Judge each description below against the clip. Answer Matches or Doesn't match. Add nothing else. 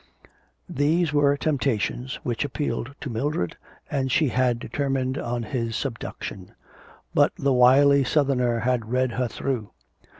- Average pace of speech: Doesn't match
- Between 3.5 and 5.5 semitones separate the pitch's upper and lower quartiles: Doesn't match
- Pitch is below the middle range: Matches